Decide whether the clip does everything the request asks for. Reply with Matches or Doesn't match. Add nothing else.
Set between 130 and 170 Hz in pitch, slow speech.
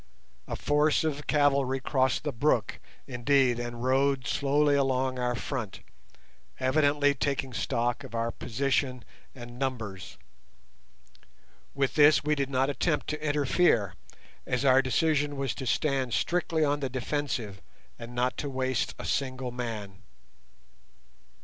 Matches